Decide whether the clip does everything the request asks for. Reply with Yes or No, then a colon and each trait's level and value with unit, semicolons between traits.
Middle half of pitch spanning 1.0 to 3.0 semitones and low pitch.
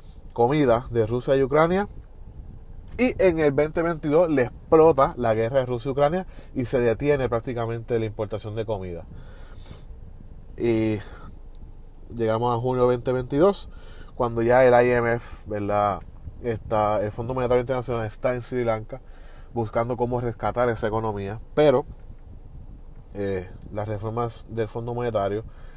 No: average, 3.6 semitones; low, 115 Hz